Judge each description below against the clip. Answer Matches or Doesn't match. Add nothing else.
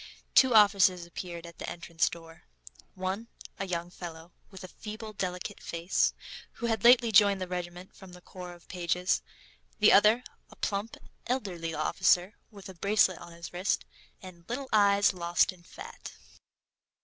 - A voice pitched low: Doesn't match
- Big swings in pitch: Doesn't match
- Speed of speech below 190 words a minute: Matches